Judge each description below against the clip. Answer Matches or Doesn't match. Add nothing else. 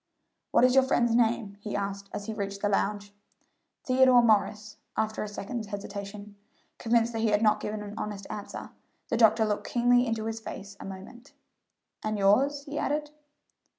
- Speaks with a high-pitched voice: Matches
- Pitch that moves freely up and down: Doesn't match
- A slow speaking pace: Doesn't match